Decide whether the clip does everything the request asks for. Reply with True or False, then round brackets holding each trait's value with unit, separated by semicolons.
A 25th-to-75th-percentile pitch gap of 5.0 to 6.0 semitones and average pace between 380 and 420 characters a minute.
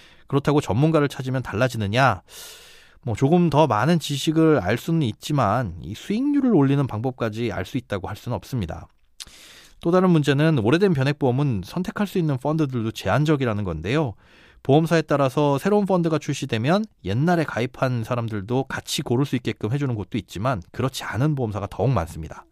True (5.4 semitones; 390 characters per minute)